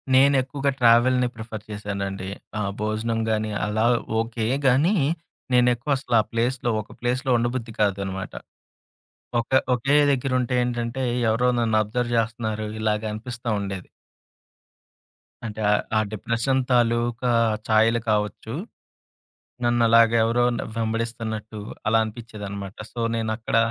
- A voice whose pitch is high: No, low, 115 Hz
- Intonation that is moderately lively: No, narrow, 2.1 semitones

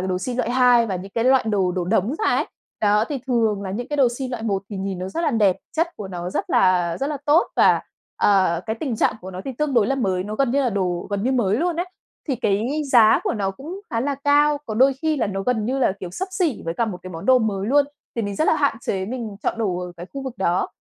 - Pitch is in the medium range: No, high, 225 Hz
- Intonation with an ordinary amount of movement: No, wide, 5.7 semitones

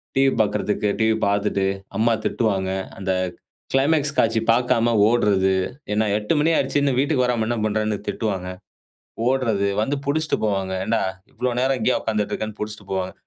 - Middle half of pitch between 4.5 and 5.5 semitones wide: No, average, 3.6 semitones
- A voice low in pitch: Yes, low, 110 Hz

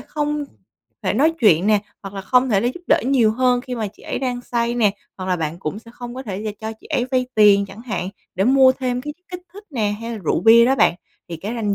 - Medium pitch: No, high, 235 Hz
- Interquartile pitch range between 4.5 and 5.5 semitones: No, average, 4.0 semitones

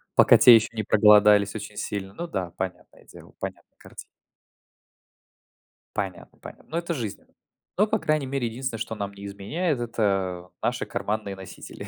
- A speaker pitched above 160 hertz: No, low, 105 Hz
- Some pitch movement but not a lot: Yes, average, 4.7 semitones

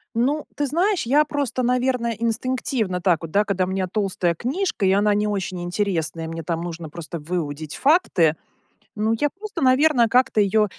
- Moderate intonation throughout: No, wide, 6.6 semitones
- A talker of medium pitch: No, high, 210 Hz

